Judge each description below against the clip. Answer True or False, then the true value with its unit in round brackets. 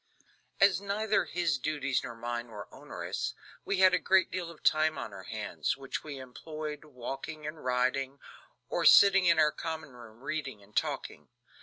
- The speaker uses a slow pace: False (170 wpm)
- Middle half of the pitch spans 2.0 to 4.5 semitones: False (5.1 semitones)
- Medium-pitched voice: True (150 Hz)